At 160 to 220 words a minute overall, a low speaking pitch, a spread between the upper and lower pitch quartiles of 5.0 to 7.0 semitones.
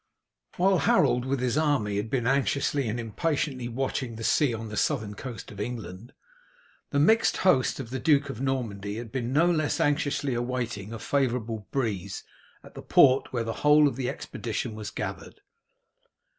No: average, 170 wpm; low, 125 Hz; average, 3.9 semitones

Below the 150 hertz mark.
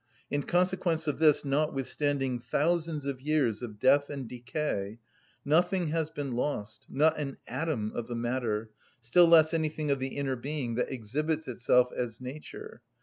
Yes: medium, 140 Hz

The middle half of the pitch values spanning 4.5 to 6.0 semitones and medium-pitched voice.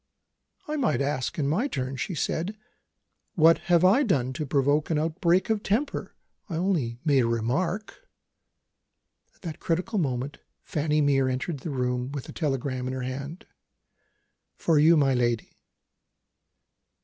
Yes: average, 5.2 semitones; medium, 150 Hz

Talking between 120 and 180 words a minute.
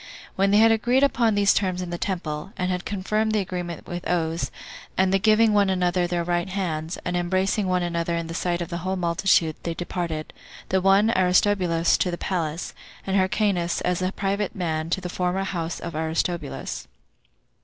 No: average, 190 wpm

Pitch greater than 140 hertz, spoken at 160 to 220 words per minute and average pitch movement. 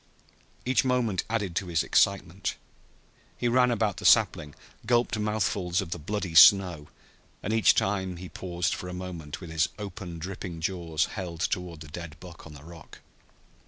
No: very low, 90 Hz; average, 165 wpm; average, 3.5 semitones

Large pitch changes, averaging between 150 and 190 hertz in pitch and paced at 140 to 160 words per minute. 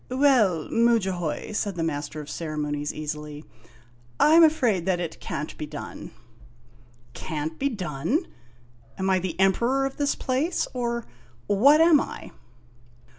Yes: wide, 8.9 semitones; medium, 185 Hz; average, 145 wpm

